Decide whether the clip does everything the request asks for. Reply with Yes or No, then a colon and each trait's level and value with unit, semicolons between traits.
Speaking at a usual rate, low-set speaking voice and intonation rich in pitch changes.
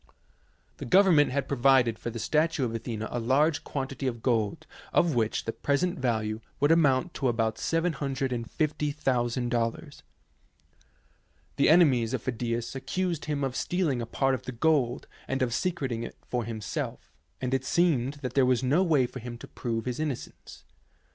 No: average, 165 wpm; low, 130 Hz; average, 3.9 semitones